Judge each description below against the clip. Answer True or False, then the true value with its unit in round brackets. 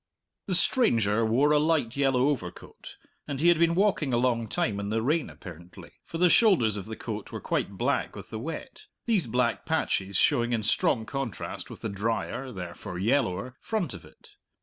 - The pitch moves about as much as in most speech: False (6.5 semitones)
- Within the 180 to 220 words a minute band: True (190 wpm)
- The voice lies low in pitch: True (120 Hz)